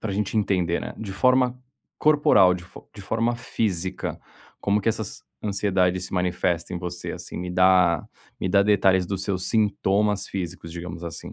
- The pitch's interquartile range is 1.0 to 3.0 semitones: Yes, average, 2.7 semitones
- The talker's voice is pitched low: Yes, very low, 95 Hz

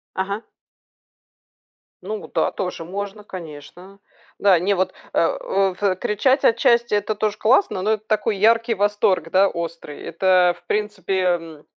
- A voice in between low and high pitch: No, high, 195 Hz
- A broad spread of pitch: No, average, 2.9 semitones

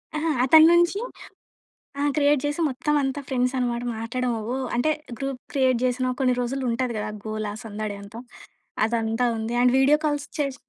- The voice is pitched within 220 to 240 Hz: No, very high, 255 Hz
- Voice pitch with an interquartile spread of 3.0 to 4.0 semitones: Yes, average, 3.5 semitones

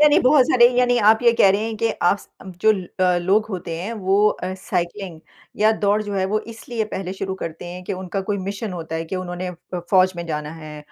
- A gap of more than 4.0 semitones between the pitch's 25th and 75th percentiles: No, average, 3.2 semitones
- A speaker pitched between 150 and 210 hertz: Yes, high, 190 Hz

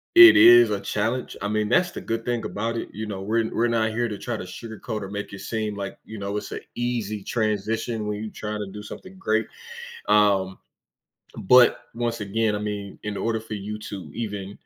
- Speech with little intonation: Yes, narrow, 2.0 semitones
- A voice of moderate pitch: No, low, 110 Hz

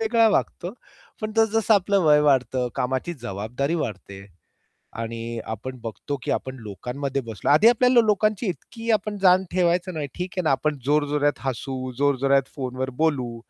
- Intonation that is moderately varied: No, wide, 6.8 semitones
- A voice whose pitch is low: No, medium, 145 Hz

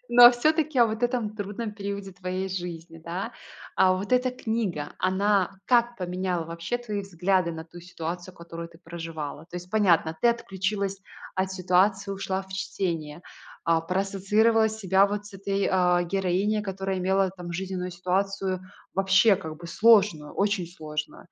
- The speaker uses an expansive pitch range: No, average, 2.8 semitones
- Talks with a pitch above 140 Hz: Yes, high, 190 Hz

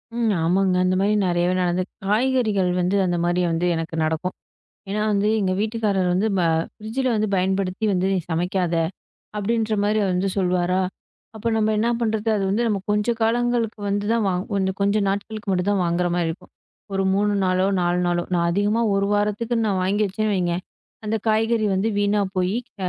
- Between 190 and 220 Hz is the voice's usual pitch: Yes, high, 200 Hz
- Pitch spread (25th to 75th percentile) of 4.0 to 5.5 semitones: No, average, 3.0 semitones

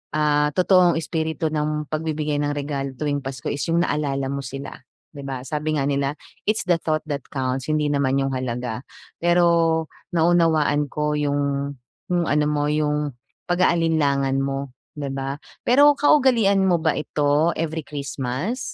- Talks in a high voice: No, medium, 150 Hz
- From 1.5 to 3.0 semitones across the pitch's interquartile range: Yes, average, 2.7 semitones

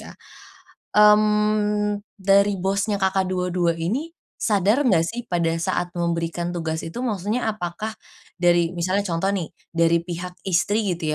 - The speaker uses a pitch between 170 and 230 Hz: Yes, high, 190 Hz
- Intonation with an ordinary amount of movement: Yes, average, 3.4 semitones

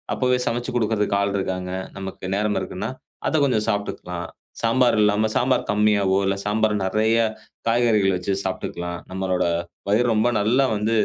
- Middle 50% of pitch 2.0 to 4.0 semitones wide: Yes, average, 3.0 semitones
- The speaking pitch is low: Yes, low, 105 Hz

